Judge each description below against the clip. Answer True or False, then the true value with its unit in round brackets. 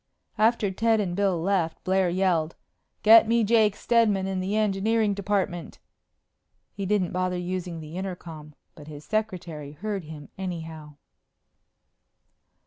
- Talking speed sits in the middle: False (130 wpm)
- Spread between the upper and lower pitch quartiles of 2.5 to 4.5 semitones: True (3.8 semitones)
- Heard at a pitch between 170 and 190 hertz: True (185 Hz)